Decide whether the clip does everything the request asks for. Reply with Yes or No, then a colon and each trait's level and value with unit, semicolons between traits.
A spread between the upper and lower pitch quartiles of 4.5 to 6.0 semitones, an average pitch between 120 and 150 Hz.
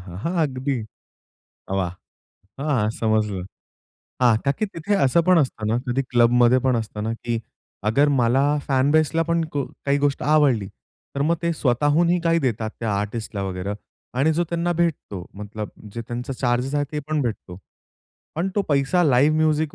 Yes: wide, 5.5 semitones; low, 135 Hz